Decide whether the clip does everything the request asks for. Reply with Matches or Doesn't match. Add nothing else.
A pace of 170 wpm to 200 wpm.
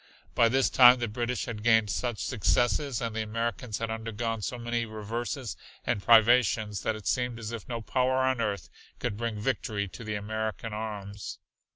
Matches